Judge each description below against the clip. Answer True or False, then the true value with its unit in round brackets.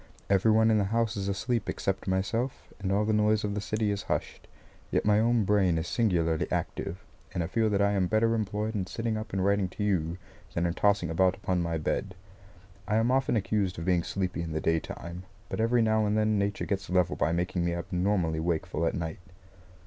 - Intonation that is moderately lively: True (3.5 semitones)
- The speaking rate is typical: False (215 wpm)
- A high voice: False (100 Hz)